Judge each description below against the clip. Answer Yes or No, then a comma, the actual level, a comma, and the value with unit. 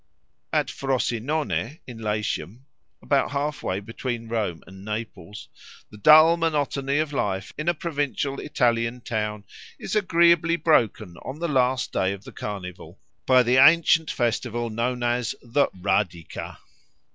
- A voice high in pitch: No, low, 125 Hz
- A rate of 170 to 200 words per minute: No, slow, 135 wpm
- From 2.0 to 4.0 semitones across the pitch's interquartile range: No, wide, 5.6 semitones